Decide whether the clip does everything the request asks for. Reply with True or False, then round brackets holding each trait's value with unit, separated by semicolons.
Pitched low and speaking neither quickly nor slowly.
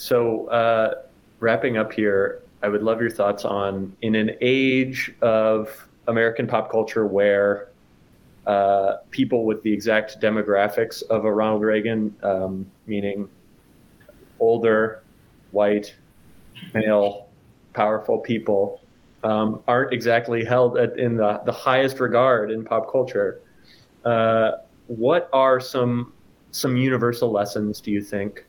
False (110 Hz; 125 wpm)